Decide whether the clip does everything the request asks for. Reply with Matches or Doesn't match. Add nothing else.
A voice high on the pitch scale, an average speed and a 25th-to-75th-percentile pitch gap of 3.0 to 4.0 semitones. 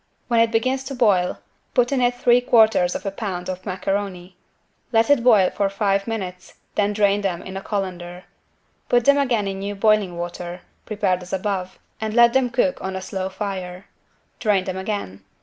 Matches